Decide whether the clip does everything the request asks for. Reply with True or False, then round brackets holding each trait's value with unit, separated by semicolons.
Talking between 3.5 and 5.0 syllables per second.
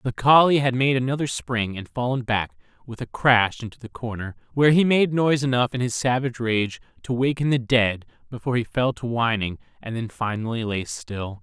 False (5.4 syllables/s)